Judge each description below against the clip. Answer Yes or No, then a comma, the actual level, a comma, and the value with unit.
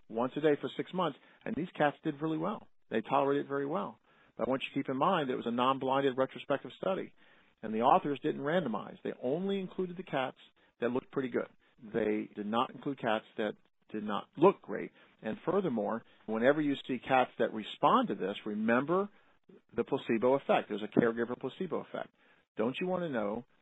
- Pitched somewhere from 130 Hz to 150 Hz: Yes, low, 135 Hz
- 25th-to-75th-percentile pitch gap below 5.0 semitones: No, average, 5.3 semitones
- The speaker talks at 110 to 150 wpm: No, average, 200 wpm